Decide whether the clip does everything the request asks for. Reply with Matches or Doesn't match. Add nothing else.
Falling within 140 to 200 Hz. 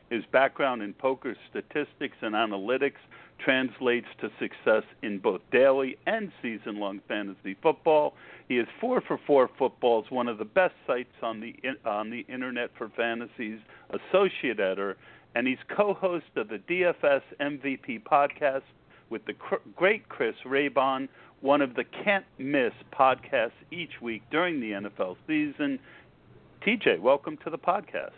Doesn't match